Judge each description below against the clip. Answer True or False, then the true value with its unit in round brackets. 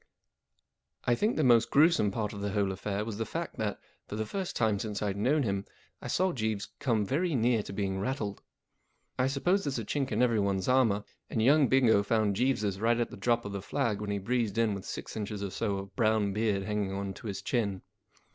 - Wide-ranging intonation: False (3.6 semitones)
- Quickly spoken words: True (225 wpm)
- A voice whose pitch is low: True (110 Hz)